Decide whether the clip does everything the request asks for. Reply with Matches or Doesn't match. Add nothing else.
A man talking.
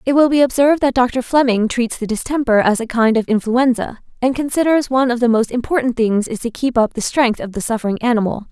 Doesn't match